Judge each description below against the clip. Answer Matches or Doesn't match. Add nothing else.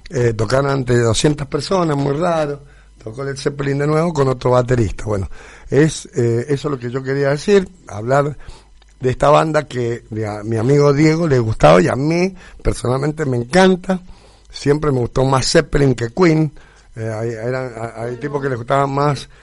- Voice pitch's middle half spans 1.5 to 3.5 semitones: Doesn't match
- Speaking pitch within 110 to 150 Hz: Matches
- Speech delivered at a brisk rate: Doesn't match